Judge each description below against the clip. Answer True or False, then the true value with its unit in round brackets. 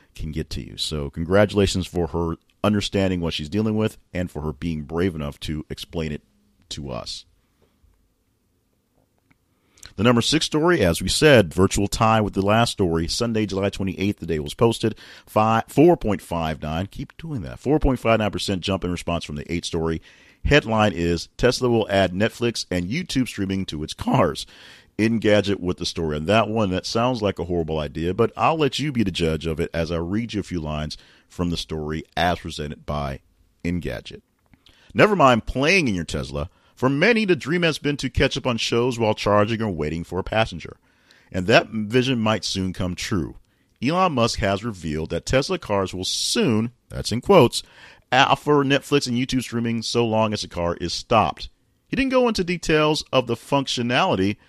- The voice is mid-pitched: False (100 Hz)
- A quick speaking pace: False (195 wpm)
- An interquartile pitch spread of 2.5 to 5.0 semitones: False (5.6 semitones)